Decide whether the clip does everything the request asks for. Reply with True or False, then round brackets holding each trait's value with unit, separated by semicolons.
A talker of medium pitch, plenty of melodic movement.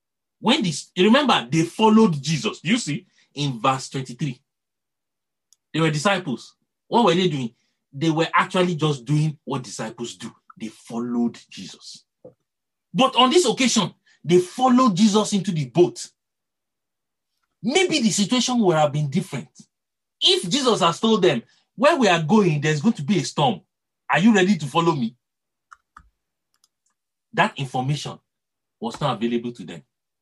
True (170 Hz; 7.6 semitones)